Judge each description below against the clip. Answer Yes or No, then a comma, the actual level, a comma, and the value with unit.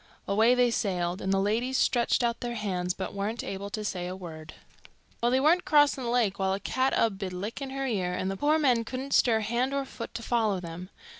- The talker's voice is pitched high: Yes, high, 220 Hz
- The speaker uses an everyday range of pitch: Yes, average, 4.6 semitones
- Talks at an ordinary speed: No, fast, 230 wpm